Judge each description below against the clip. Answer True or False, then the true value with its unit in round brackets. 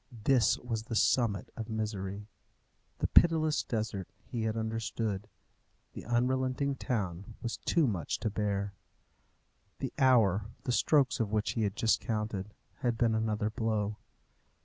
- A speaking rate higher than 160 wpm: False (140 wpm)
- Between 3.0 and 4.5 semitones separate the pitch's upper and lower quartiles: False (2.5 semitones)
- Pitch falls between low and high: False (110 Hz)